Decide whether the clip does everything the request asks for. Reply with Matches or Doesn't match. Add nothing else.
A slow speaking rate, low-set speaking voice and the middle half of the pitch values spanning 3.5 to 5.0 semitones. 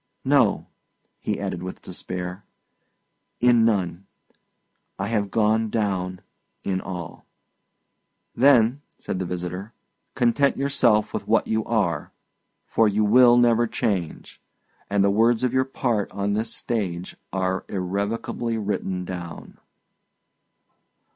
Matches